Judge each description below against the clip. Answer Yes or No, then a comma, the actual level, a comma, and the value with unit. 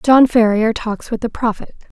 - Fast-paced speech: No, average, 180 wpm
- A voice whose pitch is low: No, high, 230 Hz